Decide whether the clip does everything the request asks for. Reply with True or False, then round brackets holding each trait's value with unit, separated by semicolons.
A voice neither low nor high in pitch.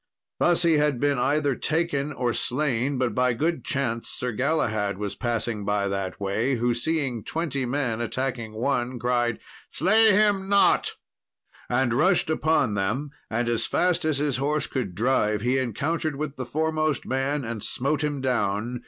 False (130 Hz)